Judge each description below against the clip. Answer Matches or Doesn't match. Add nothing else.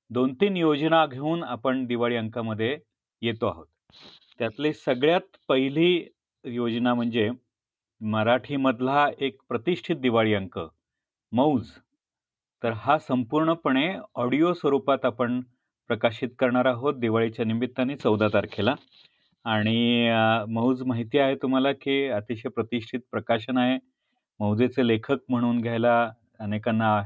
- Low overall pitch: Matches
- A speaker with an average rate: Matches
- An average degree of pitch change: Matches